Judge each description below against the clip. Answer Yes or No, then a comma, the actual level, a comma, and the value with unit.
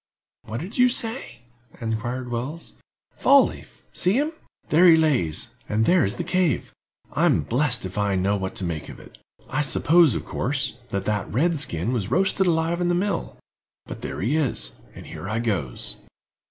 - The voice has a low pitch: Yes, low, 130 Hz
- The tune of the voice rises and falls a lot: Yes, wide, 8.6 semitones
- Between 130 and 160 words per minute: No, average, 175 wpm